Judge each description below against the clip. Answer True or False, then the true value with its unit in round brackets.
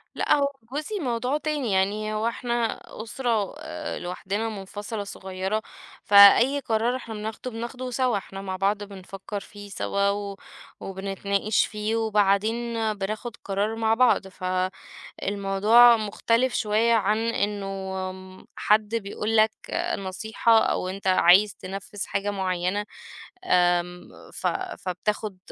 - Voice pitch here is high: True (210 Hz)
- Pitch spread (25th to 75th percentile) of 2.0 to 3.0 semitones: True (2.6 semitones)